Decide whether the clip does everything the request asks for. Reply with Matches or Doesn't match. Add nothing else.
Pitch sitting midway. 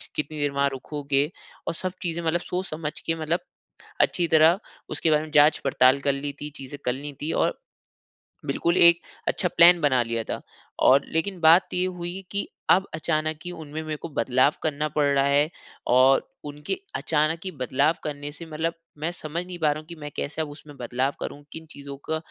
Matches